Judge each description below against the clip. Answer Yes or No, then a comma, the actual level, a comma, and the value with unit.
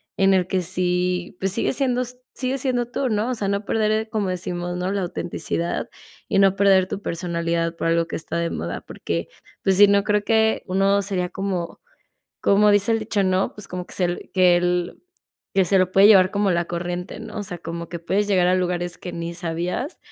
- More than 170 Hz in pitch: Yes, medium, 185 Hz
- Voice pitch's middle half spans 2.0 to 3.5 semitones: Yes, narrow, 2.6 semitones